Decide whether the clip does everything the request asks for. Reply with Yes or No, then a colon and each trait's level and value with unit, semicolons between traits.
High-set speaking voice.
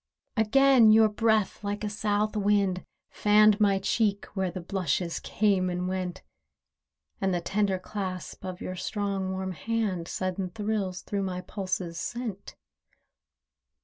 Yes: high, 200 Hz